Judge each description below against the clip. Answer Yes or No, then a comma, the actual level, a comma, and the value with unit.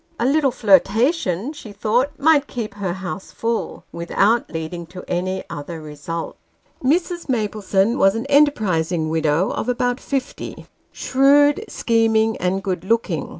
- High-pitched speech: Yes, high, 215 Hz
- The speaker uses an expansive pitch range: Yes, wide, 6.5 semitones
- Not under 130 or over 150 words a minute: Yes, slow, 135 wpm